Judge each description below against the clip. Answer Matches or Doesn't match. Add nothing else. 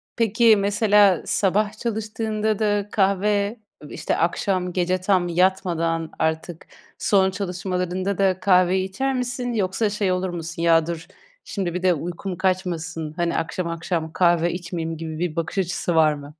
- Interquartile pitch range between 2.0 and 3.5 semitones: Matches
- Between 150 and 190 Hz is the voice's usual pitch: Matches